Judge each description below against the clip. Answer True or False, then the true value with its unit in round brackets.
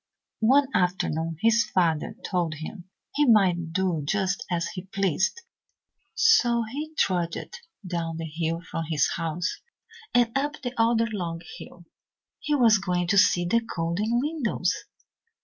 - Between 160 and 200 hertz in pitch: True (185 Hz)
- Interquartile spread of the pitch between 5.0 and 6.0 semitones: True (5.5 semitones)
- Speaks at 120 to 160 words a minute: True (140 wpm)